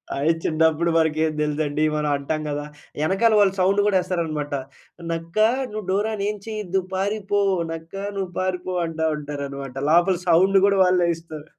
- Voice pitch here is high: No, medium, 170 Hz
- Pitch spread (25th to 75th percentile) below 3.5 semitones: No, average, 3.9 semitones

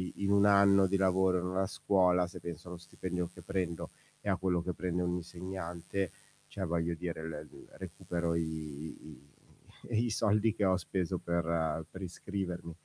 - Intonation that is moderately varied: No, narrow, 2.2 semitones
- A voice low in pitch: Yes, very low, 90 Hz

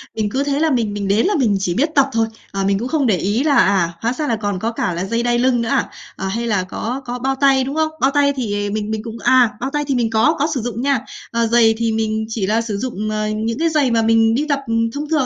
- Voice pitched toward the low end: No, high, 230 Hz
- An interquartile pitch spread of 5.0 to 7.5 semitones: No, average, 3.9 semitones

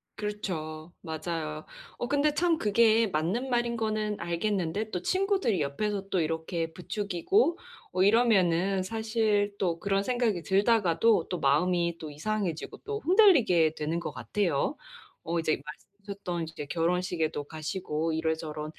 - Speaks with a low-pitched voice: No, medium, 185 Hz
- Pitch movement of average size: Yes, average, 5.0 semitones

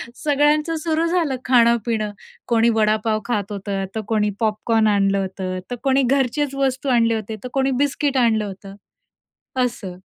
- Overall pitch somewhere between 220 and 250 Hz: Yes, high, 230 Hz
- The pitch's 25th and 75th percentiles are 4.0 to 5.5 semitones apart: Yes, average, 4.3 semitones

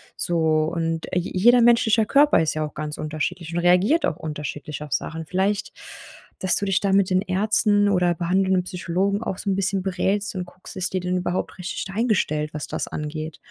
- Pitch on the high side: No, medium, 180 Hz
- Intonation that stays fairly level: No, average, 3.5 semitones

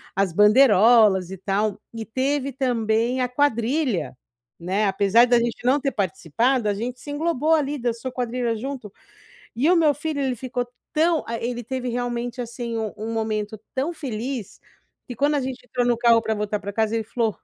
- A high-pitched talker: Yes, high, 240 Hz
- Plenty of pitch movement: No, average, 3.3 semitones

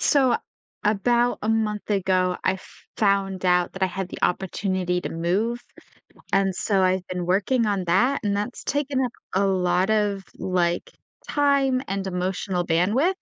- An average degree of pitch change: Yes, average, 3.4 semitones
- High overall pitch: Yes, high, 195 Hz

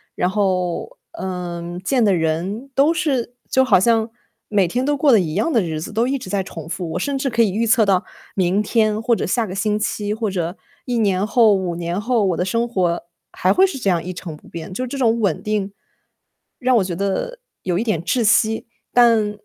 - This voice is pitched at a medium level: No, high, 210 Hz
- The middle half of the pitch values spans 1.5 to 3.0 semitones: No, average, 4.4 semitones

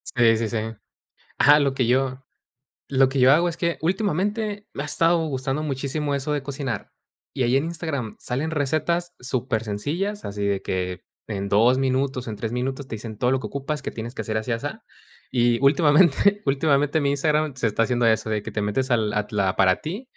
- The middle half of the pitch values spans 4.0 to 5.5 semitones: Yes, average, 4.8 semitones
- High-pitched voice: No, low, 135 Hz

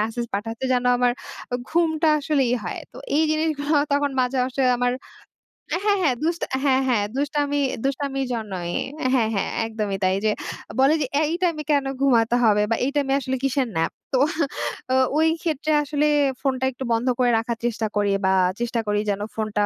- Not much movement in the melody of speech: No, average, 4.3 semitones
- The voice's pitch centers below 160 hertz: No, very high, 260 Hz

